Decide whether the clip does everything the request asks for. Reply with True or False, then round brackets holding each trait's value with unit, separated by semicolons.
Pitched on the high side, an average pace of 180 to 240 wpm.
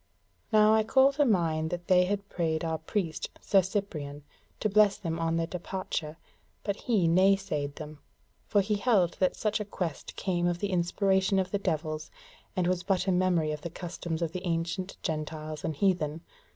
False (180 Hz; 185 wpm)